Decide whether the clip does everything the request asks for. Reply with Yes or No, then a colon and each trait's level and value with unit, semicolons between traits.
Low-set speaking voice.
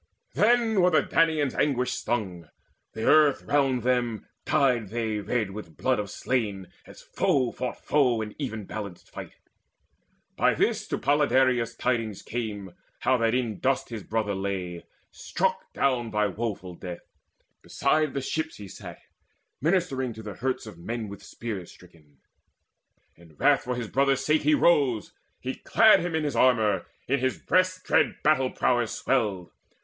Yes: low, 120 Hz